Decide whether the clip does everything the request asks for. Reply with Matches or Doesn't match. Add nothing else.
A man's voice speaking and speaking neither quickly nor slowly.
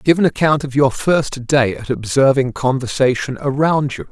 Matches